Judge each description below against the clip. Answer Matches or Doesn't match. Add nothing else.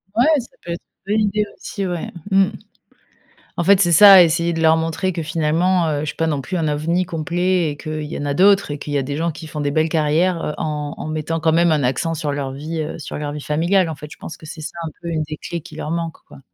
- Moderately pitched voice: Matches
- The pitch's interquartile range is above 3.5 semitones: Doesn't match